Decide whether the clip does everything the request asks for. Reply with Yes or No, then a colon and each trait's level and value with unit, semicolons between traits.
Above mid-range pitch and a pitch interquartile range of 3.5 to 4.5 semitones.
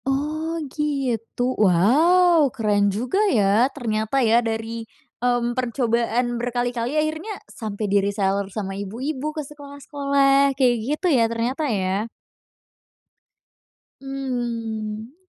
Yes: high, 245 Hz; average, 4.2 semitones